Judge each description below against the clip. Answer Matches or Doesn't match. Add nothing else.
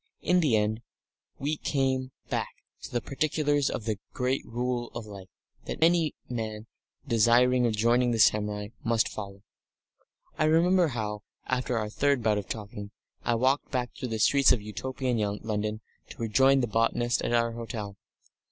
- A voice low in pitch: Matches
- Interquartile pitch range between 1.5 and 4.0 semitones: Matches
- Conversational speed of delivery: Matches